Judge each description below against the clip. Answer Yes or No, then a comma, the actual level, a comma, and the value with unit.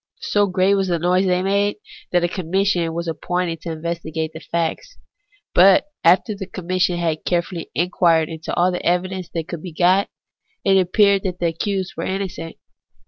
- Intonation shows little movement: Yes, narrow, 2.2 semitones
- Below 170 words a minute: No, average, 180 wpm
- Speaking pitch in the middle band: Yes, medium, 180 Hz